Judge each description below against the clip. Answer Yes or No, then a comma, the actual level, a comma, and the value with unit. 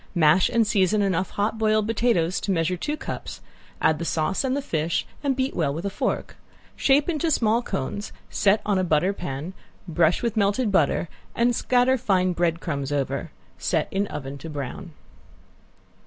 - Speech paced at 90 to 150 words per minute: No, average, 175 wpm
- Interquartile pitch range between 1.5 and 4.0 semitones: No, wide, 5.5 semitones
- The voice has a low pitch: No, high, 190 Hz